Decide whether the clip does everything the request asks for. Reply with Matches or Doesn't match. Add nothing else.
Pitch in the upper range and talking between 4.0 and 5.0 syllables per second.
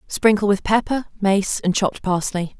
Matches